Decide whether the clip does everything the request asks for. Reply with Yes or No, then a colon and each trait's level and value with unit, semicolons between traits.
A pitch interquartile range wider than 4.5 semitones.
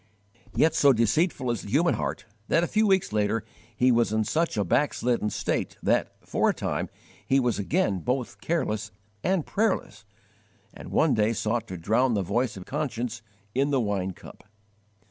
Yes: wide, 5.5 semitones